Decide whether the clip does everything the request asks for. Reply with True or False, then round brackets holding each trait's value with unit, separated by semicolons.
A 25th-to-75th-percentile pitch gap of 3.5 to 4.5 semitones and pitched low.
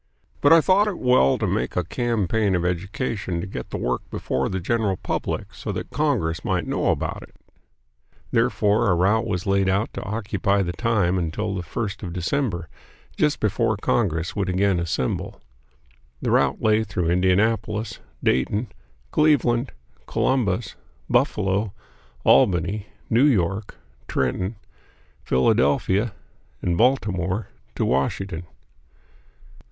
True (4.2 semitones; 100 Hz)